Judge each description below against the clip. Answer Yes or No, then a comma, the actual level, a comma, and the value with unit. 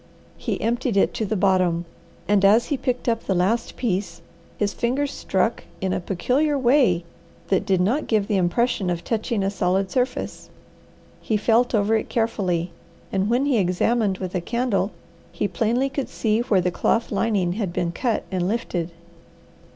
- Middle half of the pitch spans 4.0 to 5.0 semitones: Yes, average, 4.3 semitones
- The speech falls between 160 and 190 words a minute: Yes, average, 175 wpm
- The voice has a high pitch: Yes, high, 210 Hz